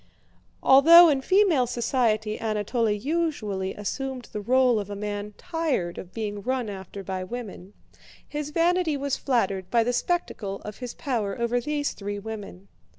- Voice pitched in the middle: No, high, 230 Hz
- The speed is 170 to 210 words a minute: No, average, 150 wpm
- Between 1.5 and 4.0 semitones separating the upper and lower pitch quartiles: No, average, 5.1 semitones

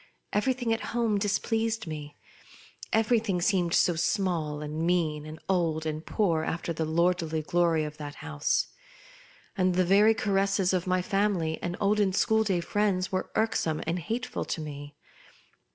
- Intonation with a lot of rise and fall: No, average, 4.6 semitones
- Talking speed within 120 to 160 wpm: Yes, average, 150 wpm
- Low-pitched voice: No, medium, 180 Hz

